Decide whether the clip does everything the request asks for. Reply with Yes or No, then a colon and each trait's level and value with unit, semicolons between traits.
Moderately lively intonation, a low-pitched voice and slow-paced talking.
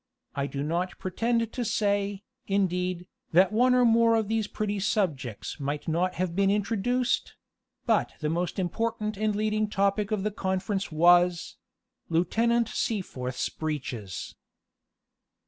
No: average, 3.8 semitones; high, 195 Hz; slow, 130 wpm